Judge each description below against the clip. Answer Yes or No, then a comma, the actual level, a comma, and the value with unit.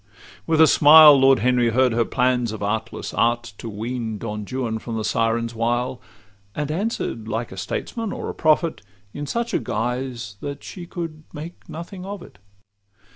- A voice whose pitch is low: Yes, low, 125 Hz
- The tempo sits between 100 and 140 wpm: No, average, 170 wpm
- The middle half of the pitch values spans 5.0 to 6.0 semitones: Yes, average, 5.3 semitones